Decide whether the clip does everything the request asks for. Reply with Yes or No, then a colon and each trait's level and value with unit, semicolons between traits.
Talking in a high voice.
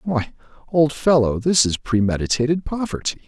No: low, 135 Hz